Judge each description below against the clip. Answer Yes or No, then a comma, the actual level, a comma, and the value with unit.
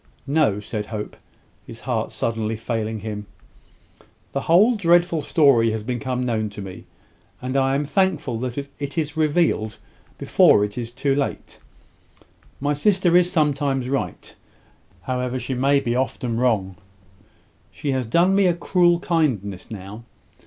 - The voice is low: Yes, low, 130 Hz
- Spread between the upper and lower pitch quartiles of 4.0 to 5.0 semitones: No, wide, 5.6 semitones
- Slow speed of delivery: No, average, 145 wpm